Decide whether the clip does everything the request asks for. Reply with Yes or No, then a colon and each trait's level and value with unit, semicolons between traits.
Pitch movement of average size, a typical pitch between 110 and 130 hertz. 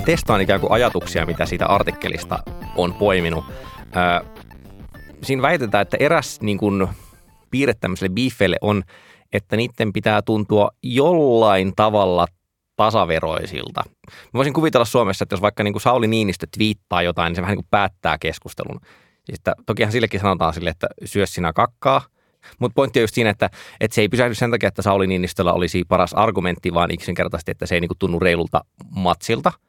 No: average, 3.7 semitones; low, 100 Hz